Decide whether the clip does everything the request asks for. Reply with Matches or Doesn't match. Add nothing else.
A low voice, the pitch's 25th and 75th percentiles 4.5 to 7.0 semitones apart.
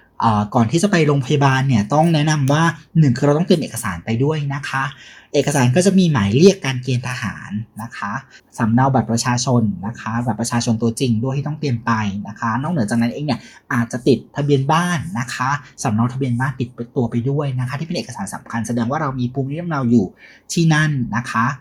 Doesn't match